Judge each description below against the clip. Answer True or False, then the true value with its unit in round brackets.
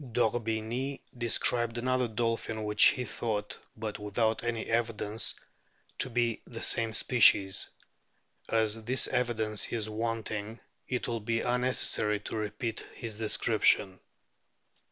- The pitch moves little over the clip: True (1.8 semitones)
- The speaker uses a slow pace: True (115 wpm)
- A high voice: False (115 Hz)